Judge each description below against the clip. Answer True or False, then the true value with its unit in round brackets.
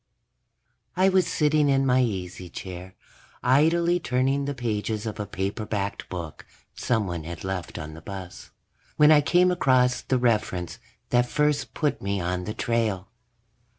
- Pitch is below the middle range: True (115 Hz)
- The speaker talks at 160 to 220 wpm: False (150 wpm)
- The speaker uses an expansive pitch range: True (6.9 semitones)